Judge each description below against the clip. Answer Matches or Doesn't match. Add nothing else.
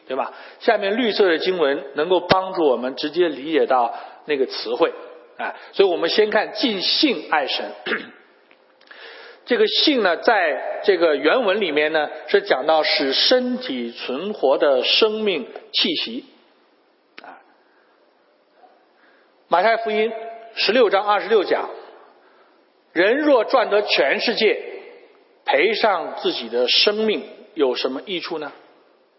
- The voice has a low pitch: Doesn't match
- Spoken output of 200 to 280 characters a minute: Doesn't match